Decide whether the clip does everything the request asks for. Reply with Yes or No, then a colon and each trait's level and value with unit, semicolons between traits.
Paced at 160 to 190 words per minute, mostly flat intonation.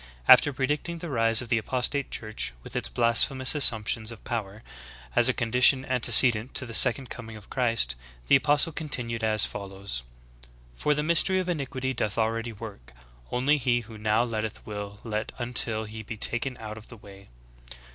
No: average, 175 wpm; average, 3.3 semitones